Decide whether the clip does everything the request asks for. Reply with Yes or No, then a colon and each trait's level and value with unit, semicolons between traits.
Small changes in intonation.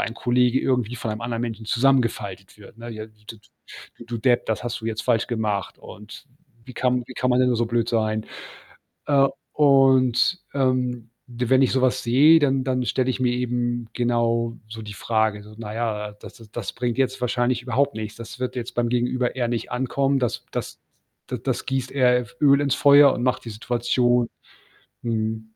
Yes: narrow, 2.1 semitones